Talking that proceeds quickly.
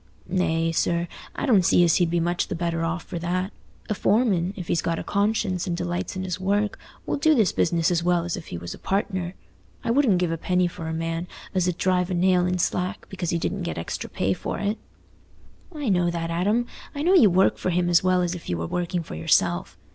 Yes: fast, 240 wpm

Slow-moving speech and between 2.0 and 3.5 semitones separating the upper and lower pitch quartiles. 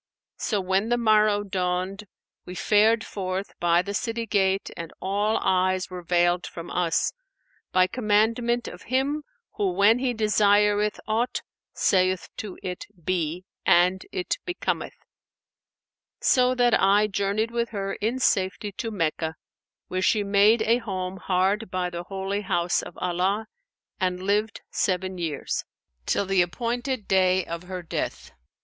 No: average, 145 wpm; average, 2.9 semitones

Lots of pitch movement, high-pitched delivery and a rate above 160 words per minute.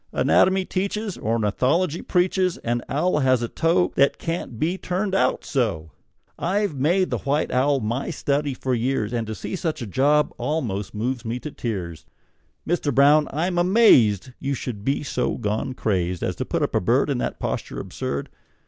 No: wide, 6.9 semitones; medium, 140 Hz; average, 175 wpm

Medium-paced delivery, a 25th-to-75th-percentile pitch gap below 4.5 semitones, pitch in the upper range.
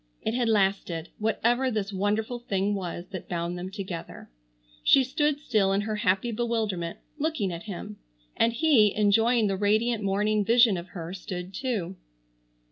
Yes: average, 155 wpm; average, 3.6 semitones; high, 205 Hz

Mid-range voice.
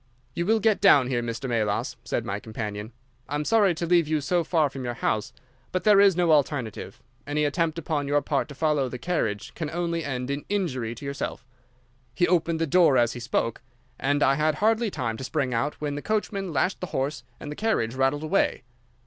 Yes: medium, 145 Hz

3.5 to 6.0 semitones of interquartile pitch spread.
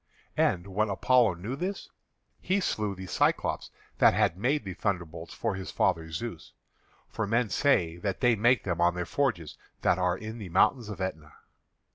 Yes: average, 5.0 semitones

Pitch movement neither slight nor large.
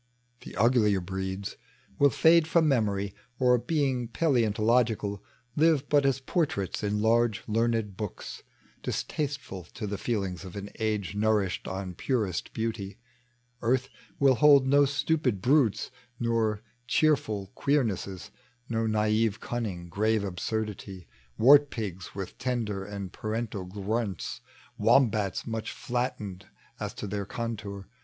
Yes: average, 4.0 semitones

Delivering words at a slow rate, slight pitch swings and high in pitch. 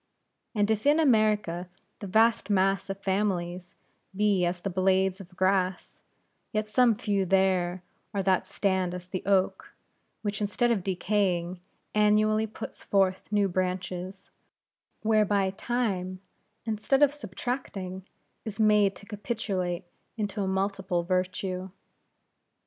Yes: slow, 125 wpm; narrow, 2.3 semitones; high, 195 Hz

